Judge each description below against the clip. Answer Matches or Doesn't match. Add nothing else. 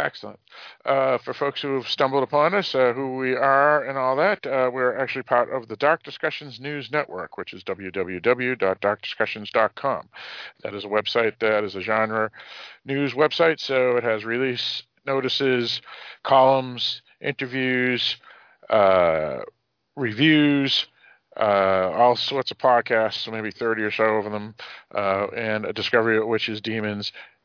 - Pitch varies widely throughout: Doesn't match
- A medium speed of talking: Matches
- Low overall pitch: Matches